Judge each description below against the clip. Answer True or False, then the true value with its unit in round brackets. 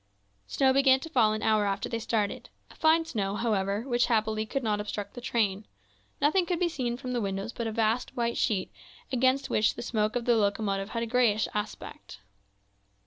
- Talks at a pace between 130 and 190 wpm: False (200 wpm)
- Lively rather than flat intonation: False (3.2 semitones)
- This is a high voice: True (225 Hz)